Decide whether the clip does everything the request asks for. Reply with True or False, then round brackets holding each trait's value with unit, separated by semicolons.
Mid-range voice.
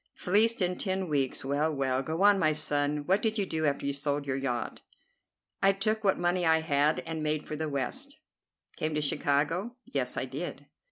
True (155 Hz)